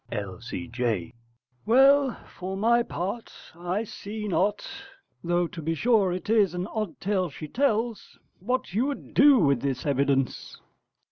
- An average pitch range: No, wide, 7.2 semitones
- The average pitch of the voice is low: No, high, 190 Hz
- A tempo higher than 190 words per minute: No, average, 140 wpm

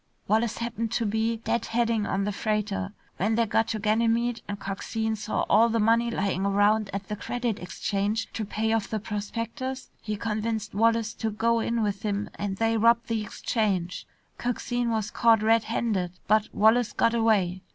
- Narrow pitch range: Yes, narrow, 1.9 semitones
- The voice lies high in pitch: Yes, high, 220 Hz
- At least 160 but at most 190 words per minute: Yes, average, 180 wpm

